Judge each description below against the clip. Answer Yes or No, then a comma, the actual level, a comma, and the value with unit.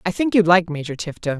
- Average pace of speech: No, fast, 260 wpm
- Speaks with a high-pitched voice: No, medium, 175 Hz